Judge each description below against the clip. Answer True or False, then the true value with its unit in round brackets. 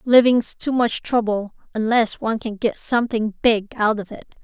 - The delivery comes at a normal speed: True (175 wpm)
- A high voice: True (225 Hz)